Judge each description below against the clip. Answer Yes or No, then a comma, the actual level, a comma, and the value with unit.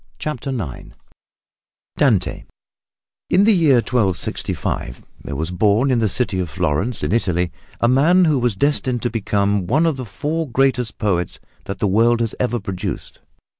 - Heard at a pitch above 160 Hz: No, low, 115 Hz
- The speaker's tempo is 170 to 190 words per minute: No, average, 160 wpm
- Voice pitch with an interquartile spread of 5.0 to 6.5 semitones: Yes, wide, 5.6 semitones